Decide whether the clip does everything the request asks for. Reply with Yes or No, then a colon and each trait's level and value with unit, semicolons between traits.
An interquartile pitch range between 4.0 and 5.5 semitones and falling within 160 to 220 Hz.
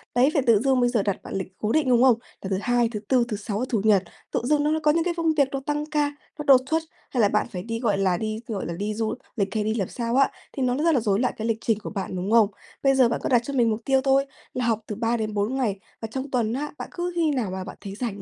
No: average, 4.3 semitones; high, 235 Hz